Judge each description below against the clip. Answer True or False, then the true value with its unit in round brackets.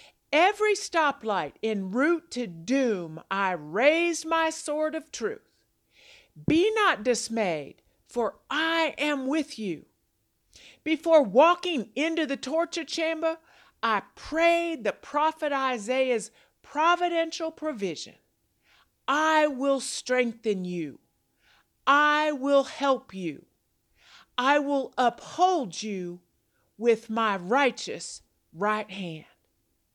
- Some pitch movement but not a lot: False (7.0 semitones)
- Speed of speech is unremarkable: False (100 wpm)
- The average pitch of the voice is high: True (275 Hz)